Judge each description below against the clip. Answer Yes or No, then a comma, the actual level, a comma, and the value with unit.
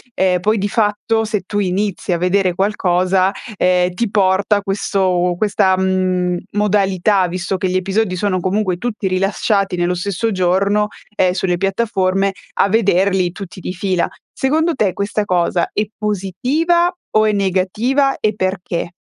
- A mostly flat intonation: Yes, narrow, 2.3 semitones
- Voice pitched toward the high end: Yes, high, 195 Hz